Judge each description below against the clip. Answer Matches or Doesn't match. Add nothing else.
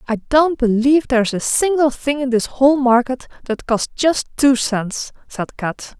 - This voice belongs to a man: Doesn't match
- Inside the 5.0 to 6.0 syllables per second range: Doesn't match